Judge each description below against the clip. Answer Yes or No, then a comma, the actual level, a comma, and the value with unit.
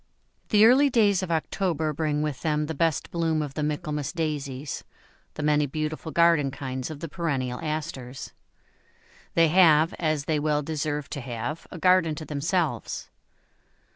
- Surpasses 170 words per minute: No, average, 155 wpm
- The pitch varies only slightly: Yes, narrow, 2.3 semitones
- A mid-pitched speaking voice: Yes, medium, 155 Hz